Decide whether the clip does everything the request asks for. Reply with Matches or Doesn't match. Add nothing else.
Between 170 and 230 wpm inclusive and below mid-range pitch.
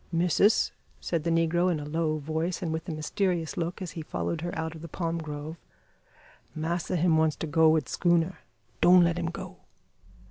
Doesn't match